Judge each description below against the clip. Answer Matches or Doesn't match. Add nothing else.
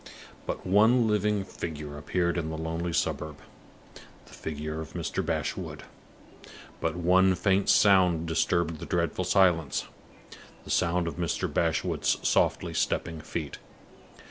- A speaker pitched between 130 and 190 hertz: Doesn't match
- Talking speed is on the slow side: Matches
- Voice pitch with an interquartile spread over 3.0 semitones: Doesn't match